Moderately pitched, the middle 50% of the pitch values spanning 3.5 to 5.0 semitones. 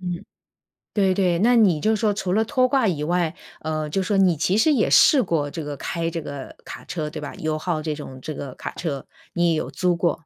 Yes: medium, 170 Hz; average, 4.2 semitones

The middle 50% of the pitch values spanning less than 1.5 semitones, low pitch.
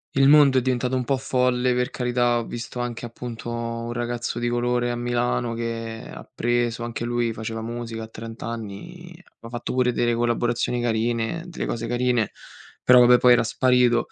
Yes: narrow, 1.1 semitones; low, 120 Hz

